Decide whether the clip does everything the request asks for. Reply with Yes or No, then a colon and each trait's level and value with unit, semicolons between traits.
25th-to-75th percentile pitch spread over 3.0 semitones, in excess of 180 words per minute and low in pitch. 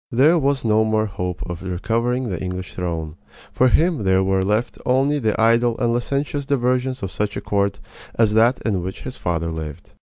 Yes: average, 5.2 semitones; average, 190 wpm; low, 110 Hz